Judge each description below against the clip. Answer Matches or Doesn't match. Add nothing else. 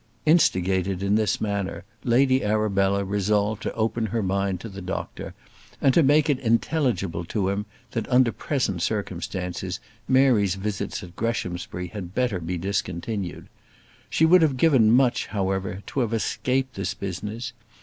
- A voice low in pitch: Matches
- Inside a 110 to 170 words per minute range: Matches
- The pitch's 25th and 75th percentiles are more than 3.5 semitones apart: Matches